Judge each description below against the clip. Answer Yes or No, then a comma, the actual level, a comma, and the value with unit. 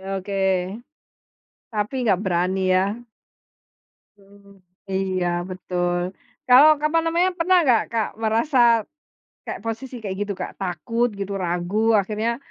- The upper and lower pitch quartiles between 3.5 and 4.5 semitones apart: Yes, average, 3.9 semitones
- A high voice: Yes, high, 210 Hz